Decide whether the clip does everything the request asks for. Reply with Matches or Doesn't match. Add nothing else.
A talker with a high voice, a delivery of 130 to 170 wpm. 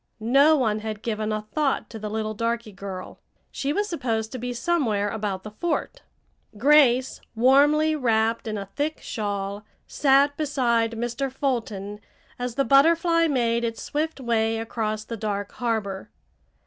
Matches